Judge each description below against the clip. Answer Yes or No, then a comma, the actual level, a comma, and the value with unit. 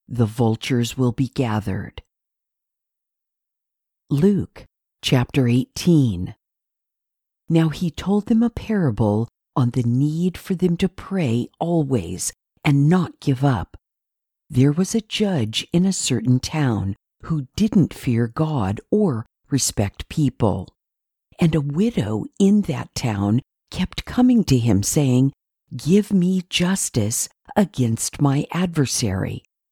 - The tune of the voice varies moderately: No, wide, 7.3 semitones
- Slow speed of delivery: Yes, slow, 115 wpm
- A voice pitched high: No, medium, 140 Hz